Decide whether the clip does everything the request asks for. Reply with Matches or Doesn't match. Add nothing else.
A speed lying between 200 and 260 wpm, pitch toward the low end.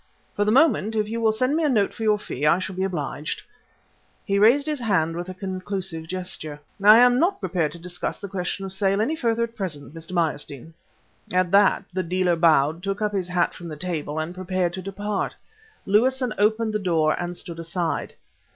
Doesn't match